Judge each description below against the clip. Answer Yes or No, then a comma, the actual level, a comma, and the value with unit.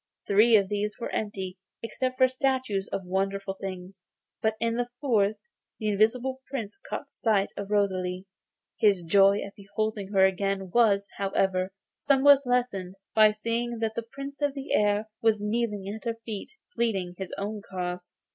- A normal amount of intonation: Yes, average, 3.3 semitones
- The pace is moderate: Yes, average, 165 wpm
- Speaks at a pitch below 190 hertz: No, high, 210 Hz